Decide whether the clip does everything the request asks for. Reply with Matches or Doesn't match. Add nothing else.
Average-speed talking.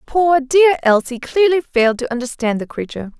Matches